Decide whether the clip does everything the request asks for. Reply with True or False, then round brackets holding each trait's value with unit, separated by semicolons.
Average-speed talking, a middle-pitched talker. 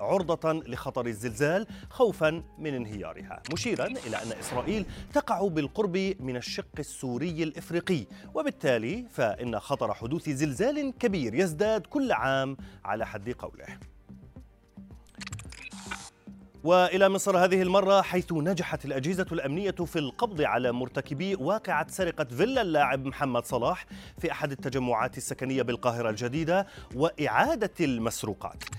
True (115 wpm; 155 Hz)